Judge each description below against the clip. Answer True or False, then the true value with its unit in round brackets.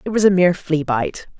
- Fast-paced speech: True (260 wpm)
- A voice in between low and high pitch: True (175 Hz)